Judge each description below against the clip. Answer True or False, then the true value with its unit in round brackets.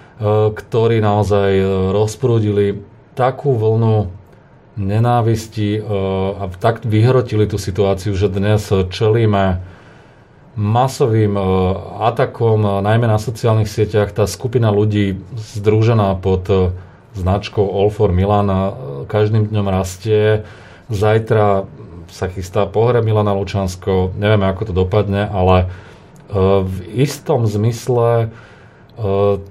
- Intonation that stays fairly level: True (2.3 semitones)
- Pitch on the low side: True (105 Hz)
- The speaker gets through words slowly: True (95 wpm)